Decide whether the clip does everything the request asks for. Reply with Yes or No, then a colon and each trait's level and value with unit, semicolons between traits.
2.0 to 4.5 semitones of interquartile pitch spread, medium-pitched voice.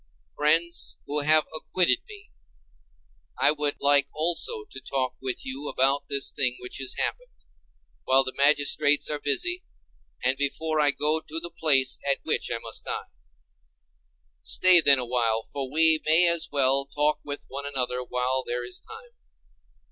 Yes: average, 3.3 semitones; medium, 145 Hz